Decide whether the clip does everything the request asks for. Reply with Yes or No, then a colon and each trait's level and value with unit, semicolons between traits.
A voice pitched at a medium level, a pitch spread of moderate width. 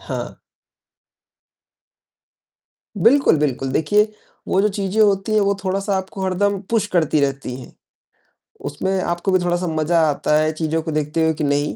Yes: medium, 175 Hz; average, 4.3 semitones